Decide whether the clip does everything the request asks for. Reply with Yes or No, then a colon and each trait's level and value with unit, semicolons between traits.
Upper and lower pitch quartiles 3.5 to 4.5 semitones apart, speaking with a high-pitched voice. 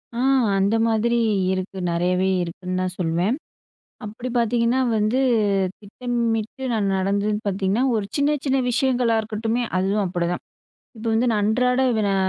Yes: average, 3.8 semitones; high, 215 Hz